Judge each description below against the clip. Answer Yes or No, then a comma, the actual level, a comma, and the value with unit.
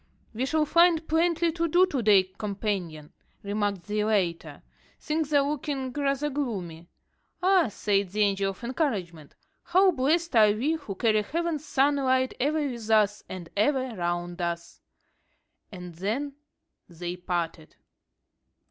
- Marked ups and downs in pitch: Yes, wide, 7.6 semitones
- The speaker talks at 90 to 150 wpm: Yes, slow, 135 wpm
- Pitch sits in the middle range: No, high, 225 Hz